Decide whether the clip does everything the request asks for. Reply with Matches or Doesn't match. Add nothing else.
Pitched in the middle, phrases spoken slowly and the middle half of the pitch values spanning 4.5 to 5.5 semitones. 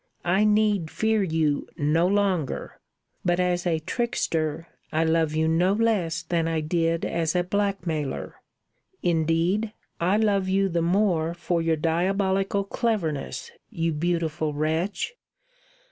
Doesn't match